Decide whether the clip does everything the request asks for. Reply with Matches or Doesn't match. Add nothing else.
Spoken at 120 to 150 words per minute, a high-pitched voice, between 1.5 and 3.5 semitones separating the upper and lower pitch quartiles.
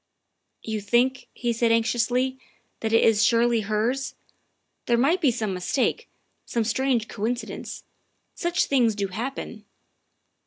Matches